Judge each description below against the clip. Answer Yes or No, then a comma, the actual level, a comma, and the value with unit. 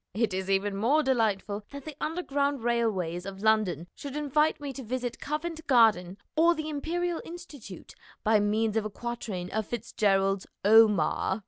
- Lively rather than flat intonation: Yes, wide, 6.1 semitones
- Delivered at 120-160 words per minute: Yes, average, 155 wpm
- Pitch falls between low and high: No, high, 225 Hz